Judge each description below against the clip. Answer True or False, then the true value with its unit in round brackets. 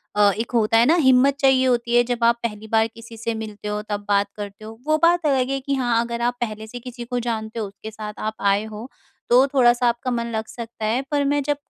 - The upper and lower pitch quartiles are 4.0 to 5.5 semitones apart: False (2.6 semitones)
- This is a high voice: True (235 Hz)